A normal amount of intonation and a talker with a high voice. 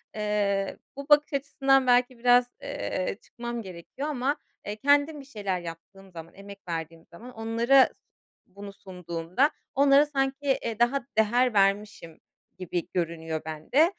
No: wide, 6.7 semitones; high, 220 Hz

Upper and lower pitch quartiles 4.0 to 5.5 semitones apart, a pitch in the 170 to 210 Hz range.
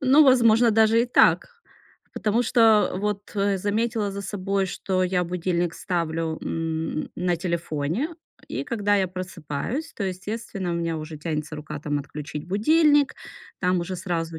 Yes: average, 4.8 semitones; medium, 185 Hz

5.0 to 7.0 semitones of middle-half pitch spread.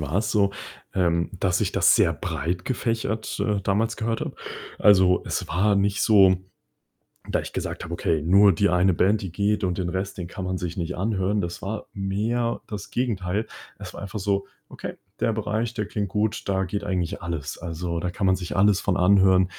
No: narrow, 2.5 semitones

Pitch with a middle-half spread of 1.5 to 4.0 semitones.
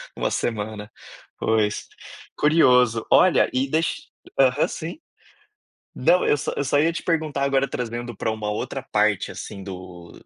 No: wide, 5.4 semitones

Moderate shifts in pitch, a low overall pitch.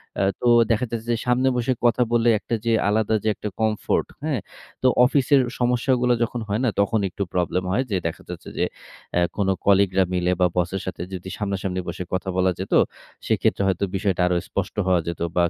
Yes: average, 4.3 semitones; low, 100 Hz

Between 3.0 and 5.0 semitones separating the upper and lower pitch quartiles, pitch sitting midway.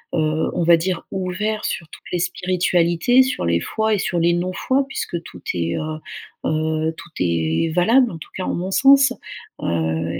Yes: average, 3.7 semitones; medium, 175 Hz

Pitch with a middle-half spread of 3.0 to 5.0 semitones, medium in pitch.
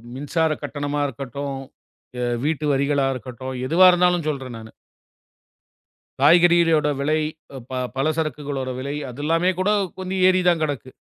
Yes: average, 3.9 semitones; medium, 150 Hz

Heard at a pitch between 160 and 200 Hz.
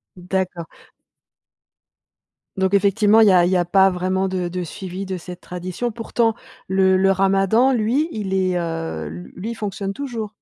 Yes: high, 190 Hz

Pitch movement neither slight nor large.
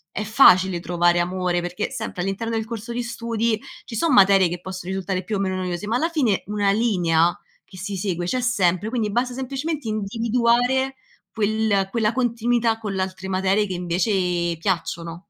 Yes: average, 4.1 semitones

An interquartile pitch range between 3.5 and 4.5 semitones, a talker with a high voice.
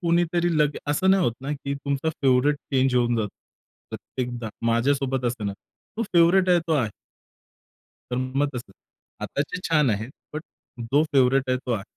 No: average, 4.2 semitones; low, 135 Hz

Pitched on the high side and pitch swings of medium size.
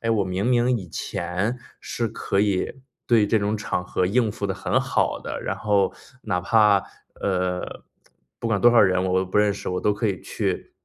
No: low, 100 Hz; average, 3.2 semitones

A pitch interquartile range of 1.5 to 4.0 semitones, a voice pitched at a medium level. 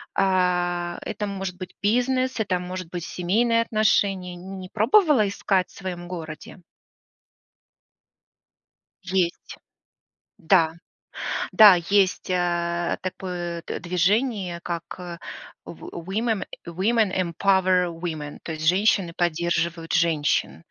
Yes: narrow, 2.5 semitones; medium, 180 Hz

